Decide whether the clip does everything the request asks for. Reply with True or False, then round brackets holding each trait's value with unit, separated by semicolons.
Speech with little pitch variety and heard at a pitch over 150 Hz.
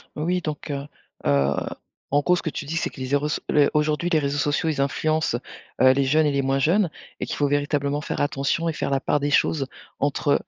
False (2.0 semitones; 145 Hz)